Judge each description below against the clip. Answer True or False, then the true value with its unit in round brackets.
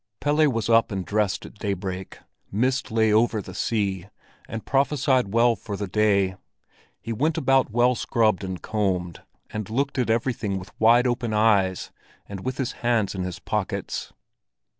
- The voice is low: True (110 Hz)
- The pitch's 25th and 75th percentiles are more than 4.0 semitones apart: False (3.7 semitones)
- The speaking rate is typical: True (160 wpm)